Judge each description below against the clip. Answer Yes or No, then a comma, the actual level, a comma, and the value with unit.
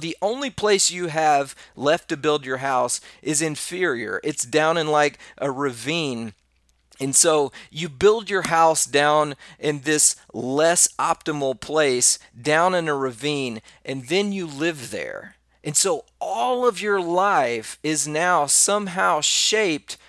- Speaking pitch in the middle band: Yes, medium, 155 Hz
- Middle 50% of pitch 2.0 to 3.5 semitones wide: No, average, 4.4 semitones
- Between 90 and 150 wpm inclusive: Yes, average, 145 wpm